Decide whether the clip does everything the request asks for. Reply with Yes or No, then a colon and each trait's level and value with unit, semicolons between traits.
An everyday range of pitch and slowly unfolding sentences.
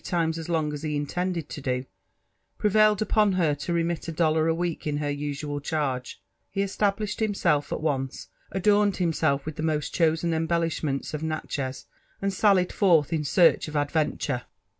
No: average, 3.4 semitones; average, 170 wpm